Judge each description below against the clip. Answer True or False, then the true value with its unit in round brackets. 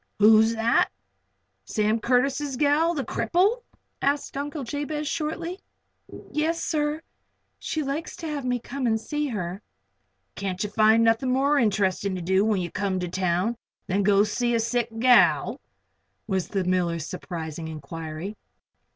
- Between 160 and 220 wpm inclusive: False (150 wpm)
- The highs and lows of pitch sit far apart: True (7.1 semitones)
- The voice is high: True (225 Hz)